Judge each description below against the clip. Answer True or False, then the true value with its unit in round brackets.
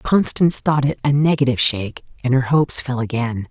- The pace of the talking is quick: False (190 wpm)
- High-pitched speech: False (130 Hz)